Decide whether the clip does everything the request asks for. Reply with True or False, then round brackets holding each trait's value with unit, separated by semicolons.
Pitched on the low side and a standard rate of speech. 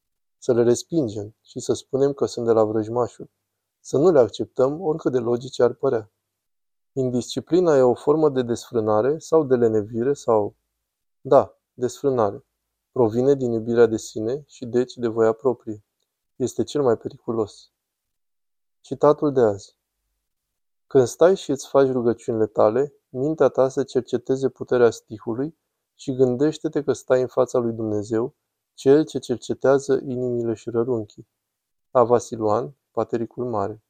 True (120 Hz; 140 wpm)